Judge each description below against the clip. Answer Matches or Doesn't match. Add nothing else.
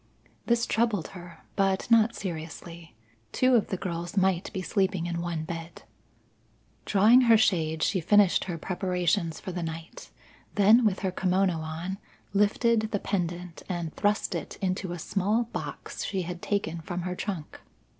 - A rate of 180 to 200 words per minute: Doesn't match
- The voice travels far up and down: Doesn't match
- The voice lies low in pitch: Doesn't match